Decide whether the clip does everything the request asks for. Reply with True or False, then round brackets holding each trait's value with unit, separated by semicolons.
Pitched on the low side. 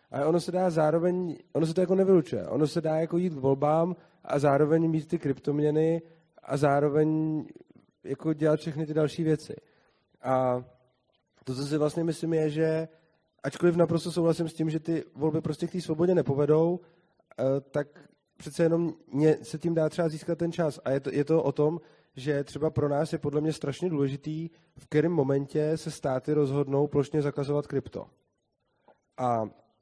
False (155 Hz)